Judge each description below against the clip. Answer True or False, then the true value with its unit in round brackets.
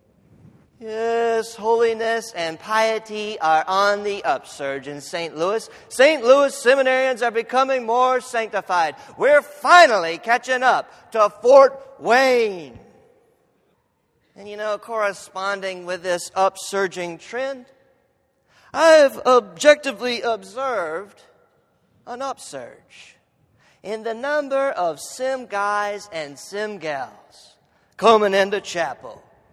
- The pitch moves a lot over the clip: False (4.8 semitones)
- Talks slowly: True (100 wpm)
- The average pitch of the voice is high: True (225 Hz)